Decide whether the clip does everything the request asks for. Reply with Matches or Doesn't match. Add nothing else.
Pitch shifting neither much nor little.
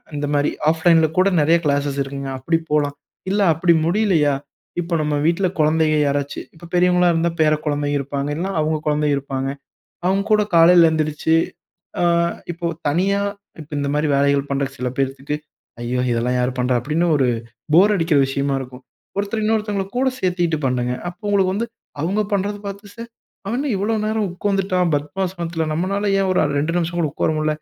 Matches